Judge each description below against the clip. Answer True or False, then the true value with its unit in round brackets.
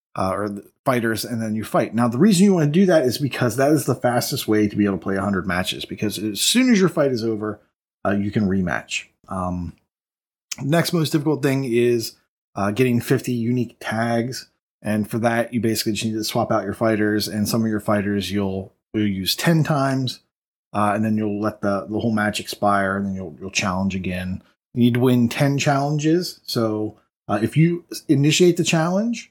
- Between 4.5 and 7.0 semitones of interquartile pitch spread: True (4.9 semitones)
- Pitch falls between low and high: False (115 Hz)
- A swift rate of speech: True (215 wpm)